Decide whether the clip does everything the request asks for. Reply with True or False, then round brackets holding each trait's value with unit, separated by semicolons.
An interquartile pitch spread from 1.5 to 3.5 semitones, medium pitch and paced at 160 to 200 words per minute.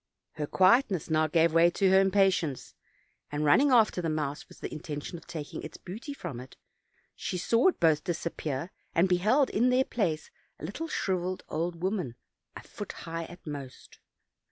False (3.9 semitones; 175 Hz; 170 wpm)